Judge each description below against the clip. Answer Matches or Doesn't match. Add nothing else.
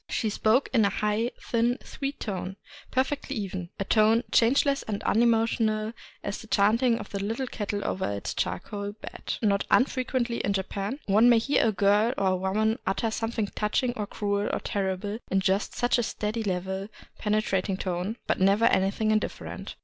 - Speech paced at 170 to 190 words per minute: Matches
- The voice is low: Doesn't match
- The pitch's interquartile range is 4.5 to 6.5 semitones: Doesn't match